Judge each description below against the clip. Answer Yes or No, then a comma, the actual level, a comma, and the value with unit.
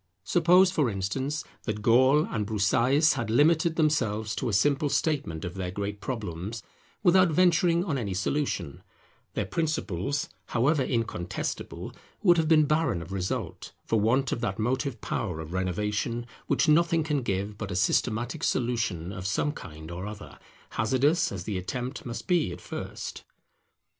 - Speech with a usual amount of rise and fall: No, wide, 7.3 semitones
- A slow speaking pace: No, average, 155 wpm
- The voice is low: Yes, low, 120 Hz